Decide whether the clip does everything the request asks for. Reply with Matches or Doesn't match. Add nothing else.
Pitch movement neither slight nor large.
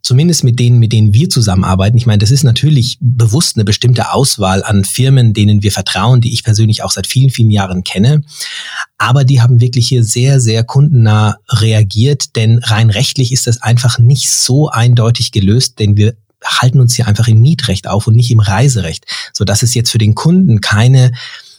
Matches